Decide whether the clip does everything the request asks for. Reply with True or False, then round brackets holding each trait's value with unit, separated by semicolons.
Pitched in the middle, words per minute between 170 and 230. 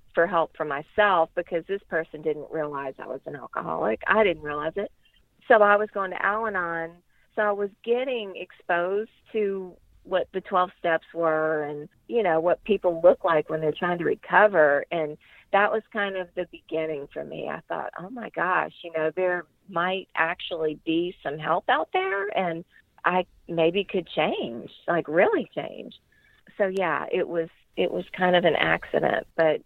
True (175 Hz; 180 wpm)